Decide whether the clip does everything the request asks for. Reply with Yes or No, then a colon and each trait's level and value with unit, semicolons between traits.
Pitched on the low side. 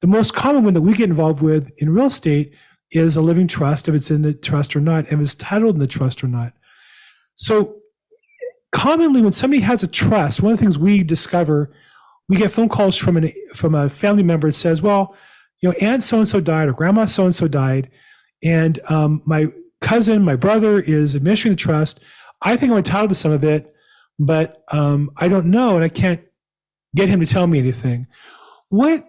No: medium, 170 Hz